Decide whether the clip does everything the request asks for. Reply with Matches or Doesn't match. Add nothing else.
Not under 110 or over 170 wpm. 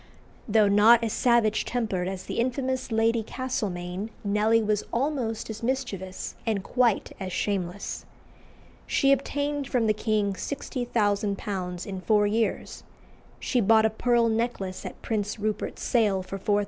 Matches